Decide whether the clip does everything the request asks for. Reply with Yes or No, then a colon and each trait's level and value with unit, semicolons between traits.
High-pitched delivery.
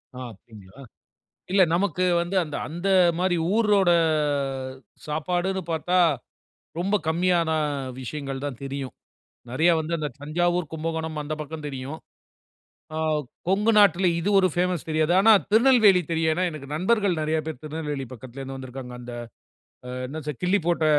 No: medium, 160 Hz